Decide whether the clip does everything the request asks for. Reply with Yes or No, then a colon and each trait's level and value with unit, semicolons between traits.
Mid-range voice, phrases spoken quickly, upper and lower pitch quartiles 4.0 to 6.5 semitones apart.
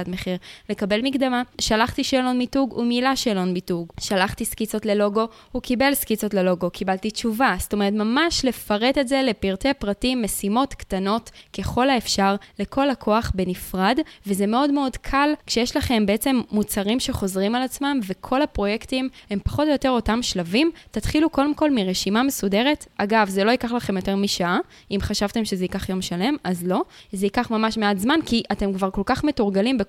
No: high, 220 Hz; fast, 165 wpm; average, 4.6 semitones